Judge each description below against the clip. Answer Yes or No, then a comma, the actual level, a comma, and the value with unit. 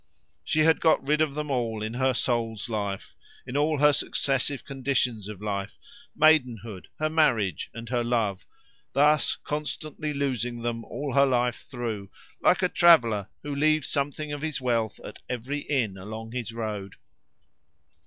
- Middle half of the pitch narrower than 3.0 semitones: No, average, 4.7 semitones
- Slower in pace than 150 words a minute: No, average, 155 wpm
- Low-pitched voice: Yes, low, 125 Hz